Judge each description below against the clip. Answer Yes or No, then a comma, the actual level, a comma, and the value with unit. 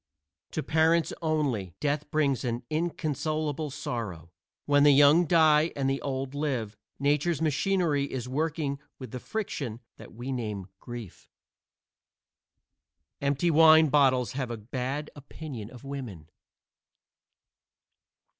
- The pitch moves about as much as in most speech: Yes, average, 3.7 semitones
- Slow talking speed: Yes, slow, 115 wpm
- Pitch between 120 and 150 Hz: Yes, medium, 140 Hz